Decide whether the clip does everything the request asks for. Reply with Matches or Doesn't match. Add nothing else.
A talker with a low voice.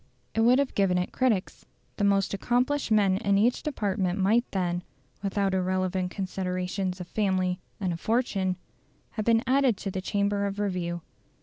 Doesn't match